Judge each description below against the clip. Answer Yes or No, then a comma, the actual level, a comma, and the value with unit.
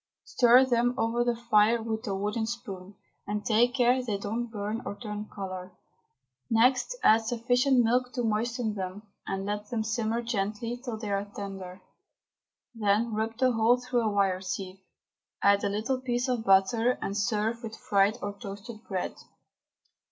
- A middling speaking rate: Yes, average, 165 wpm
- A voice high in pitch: Yes, high, 220 Hz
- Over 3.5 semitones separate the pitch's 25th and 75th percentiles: No, average, 3.0 semitones